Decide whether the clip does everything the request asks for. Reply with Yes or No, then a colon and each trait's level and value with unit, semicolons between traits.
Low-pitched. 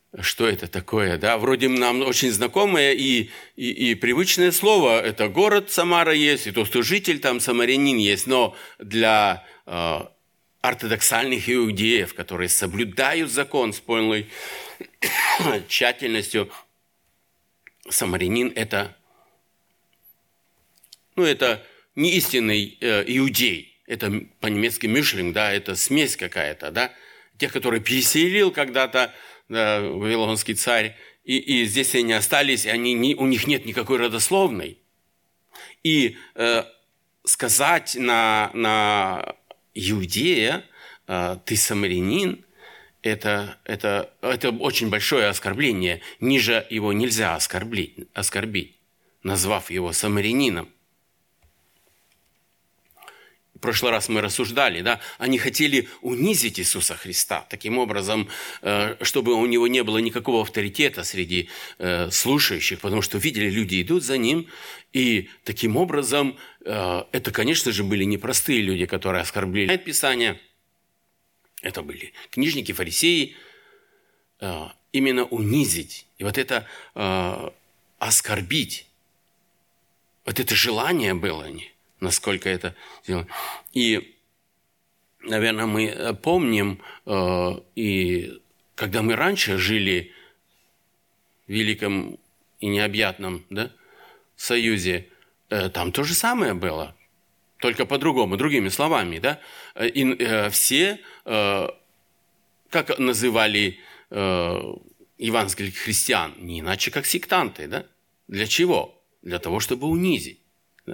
Yes: low, 110 Hz